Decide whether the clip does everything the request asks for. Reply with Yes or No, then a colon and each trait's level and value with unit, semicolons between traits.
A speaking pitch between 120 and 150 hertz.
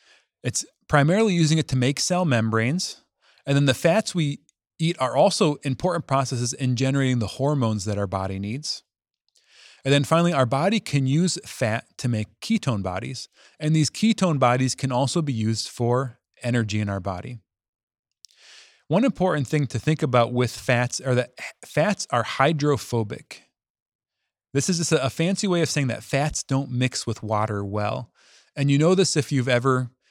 Yes: low, 135 Hz